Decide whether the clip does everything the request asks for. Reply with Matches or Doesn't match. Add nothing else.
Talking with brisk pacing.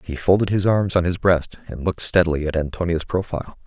Matches